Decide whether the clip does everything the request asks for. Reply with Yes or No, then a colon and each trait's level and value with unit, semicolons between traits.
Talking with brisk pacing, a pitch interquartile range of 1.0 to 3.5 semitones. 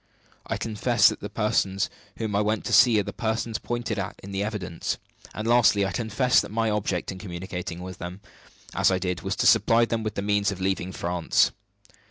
Yes: fast, 210 wpm; average, 3.0 semitones